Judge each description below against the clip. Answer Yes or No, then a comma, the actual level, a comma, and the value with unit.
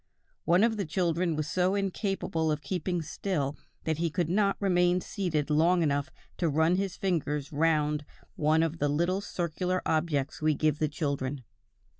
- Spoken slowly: No, average, 165 wpm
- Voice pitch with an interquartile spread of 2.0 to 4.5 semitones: Yes, average, 3.3 semitones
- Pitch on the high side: No, medium, 165 Hz